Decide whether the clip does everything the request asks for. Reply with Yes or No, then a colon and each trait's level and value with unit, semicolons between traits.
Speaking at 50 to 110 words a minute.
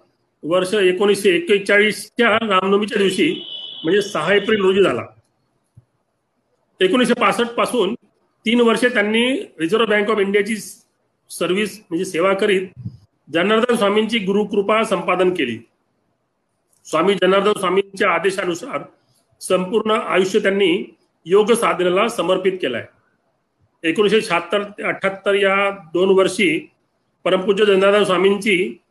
Yes: average, 100 wpm